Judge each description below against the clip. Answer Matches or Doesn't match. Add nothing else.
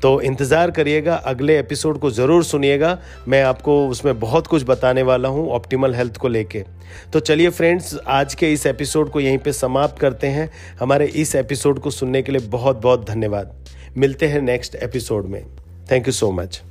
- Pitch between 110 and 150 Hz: Matches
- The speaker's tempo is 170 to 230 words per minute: Matches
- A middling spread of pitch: Matches